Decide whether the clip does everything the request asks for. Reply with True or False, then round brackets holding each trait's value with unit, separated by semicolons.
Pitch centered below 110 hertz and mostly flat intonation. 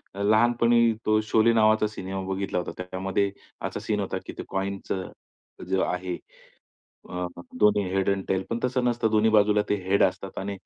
True (100 Hz; 2.3 semitones)